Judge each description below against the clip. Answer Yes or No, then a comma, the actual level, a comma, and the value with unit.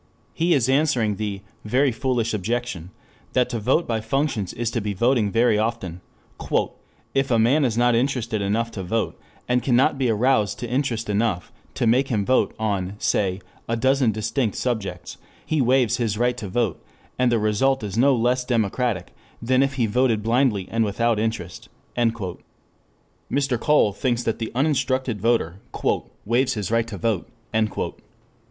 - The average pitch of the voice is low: Yes, low, 115 Hz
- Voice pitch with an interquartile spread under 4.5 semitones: Yes, average, 3.3 semitones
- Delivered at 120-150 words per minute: No, average, 160 wpm